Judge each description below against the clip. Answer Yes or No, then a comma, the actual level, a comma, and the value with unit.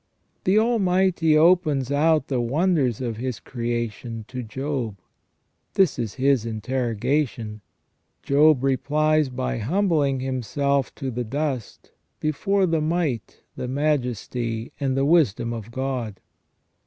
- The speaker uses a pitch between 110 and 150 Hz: Yes, low, 135 Hz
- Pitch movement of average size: Yes, average, 4.5 semitones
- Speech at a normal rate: No, slow, 120 wpm